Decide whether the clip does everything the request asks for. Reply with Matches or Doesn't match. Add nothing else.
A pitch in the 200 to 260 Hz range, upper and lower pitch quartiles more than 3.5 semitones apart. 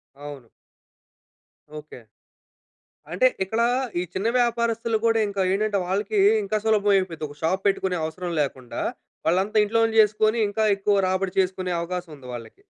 Doesn't match